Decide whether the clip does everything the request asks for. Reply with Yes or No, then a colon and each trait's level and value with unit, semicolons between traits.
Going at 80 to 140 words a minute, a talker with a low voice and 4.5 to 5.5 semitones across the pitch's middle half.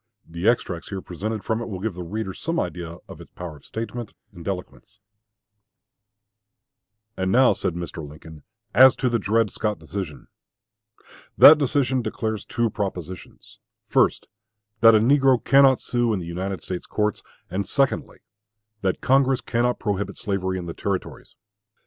No: average, 155 wpm; low, 105 Hz; average, 4.8 semitones